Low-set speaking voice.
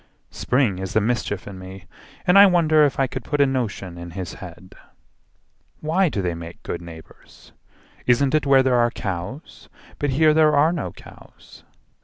Yes: low, 120 Hz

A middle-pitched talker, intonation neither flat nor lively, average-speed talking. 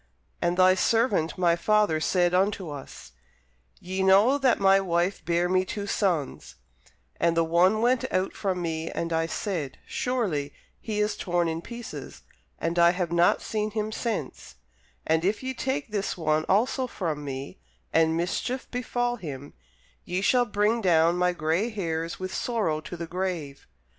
Yes: medium, 180 Hz; average, 4.4 semitones; average, 165 wpm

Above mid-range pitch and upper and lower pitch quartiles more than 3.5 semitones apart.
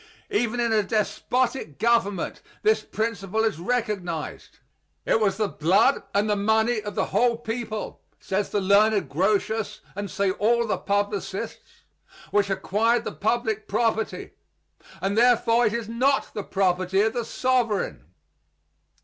No: high, 215 Hz; average, 2.8 semitones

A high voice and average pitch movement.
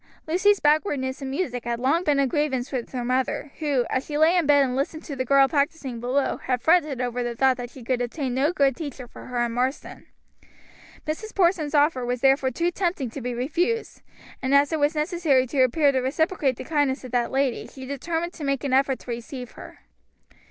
Yes: very high, 275 Hz; average, 3.3 semitones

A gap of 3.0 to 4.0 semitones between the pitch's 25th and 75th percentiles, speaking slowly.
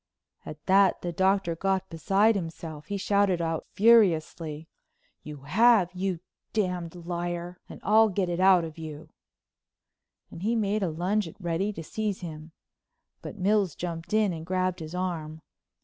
No: average, 3.3 semitones; average, 155 wpm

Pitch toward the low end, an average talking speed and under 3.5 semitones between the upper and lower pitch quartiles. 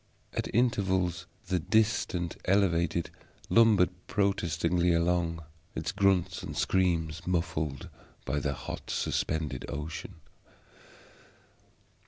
No: very low, 85 Hz; slow, 90 wpm; average, 2.8 semitones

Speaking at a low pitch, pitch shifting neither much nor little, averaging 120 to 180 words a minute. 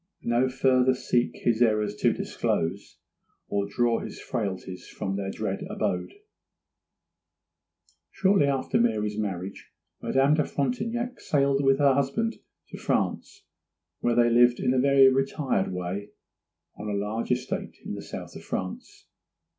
Yes: low, 120 Hz; average, 4.8 semitones; average, 140 wpm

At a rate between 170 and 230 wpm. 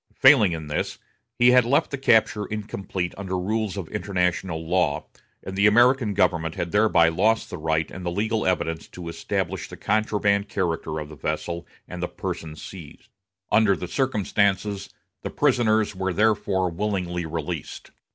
No: average, 160 wpm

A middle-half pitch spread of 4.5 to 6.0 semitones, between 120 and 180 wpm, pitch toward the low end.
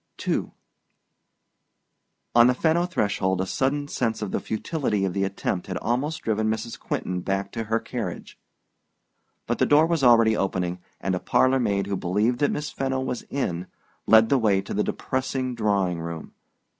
Yes: average, 5.2 semitones; average, 170 wpm; low, 110 Hz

